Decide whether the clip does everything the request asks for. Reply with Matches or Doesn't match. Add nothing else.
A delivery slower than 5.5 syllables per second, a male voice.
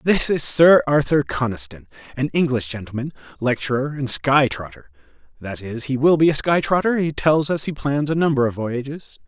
Matches